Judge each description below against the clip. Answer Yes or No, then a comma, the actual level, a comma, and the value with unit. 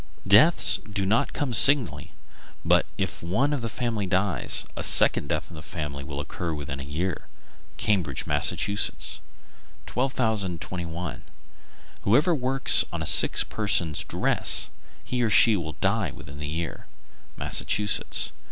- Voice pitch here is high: No, very low, 95 Hz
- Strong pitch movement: Yes, wide, 6.5 semitones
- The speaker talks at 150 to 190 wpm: No, average, 140 wpm